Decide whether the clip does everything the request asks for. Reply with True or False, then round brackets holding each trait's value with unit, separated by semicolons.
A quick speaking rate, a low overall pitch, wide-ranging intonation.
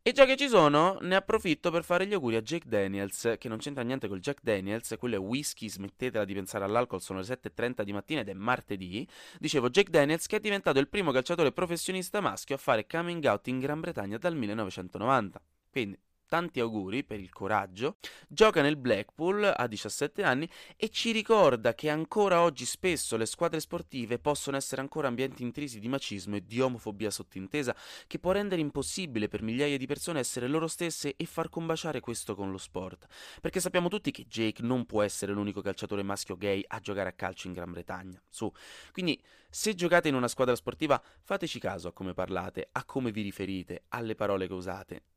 True (195 wpm; 125 Hz; 8.4 semitones)